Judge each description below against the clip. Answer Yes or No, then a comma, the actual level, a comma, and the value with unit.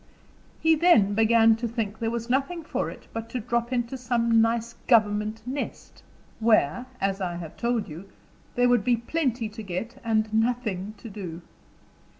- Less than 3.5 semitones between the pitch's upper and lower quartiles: Yes, narrow, 2.5 semitones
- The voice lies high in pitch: Yes, high, 230 Hz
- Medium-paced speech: Yes, average, 165 wpm